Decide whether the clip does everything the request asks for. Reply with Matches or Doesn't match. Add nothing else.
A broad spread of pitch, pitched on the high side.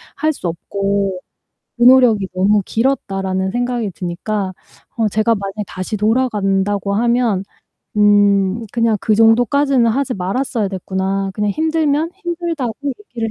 Doesn't match